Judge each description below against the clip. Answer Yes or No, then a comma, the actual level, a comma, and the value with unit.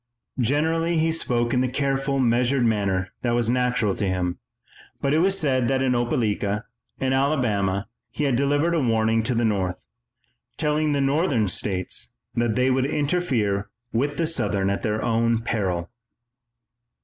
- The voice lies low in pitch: Yes, low, 125 Hz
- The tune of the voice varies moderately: Yes, average, 5.0 semitones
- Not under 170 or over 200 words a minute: No, average, 155 wpm